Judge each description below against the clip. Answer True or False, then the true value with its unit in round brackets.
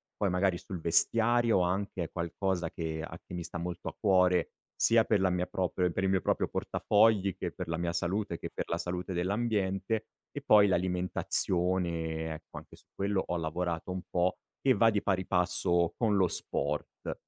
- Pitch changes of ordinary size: False (2.2 semitones)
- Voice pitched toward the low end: True (90 Hz)